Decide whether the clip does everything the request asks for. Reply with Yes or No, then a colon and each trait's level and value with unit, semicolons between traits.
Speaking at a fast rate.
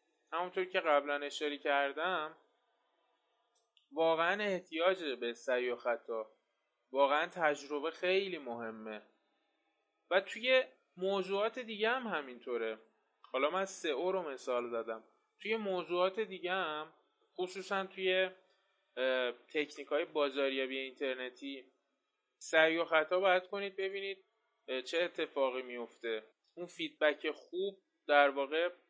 No: average, 110 wpm